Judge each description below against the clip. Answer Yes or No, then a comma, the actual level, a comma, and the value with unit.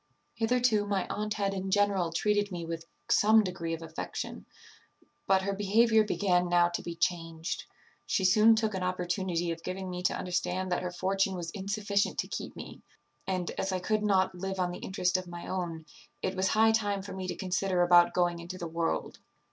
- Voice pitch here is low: No, medium, 185 Hz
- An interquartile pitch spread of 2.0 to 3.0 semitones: Yes, narrow, 2.5 semitones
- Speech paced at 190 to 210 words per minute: Yes, average, 195 wpm